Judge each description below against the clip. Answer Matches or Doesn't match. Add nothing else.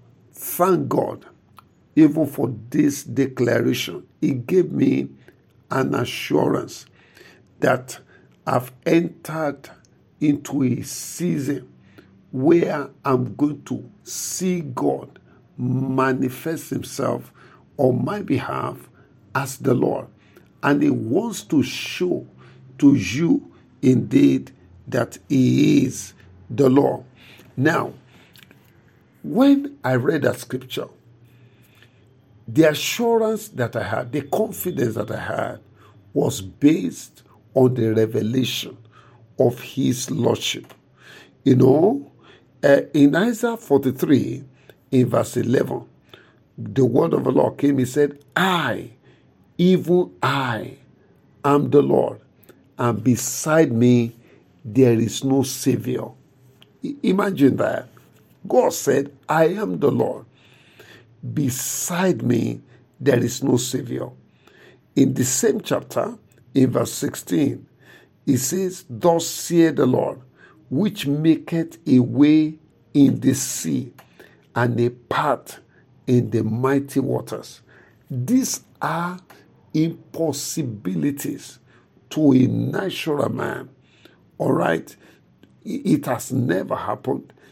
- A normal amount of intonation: Matches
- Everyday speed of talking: Doesn't match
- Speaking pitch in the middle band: Doesn't match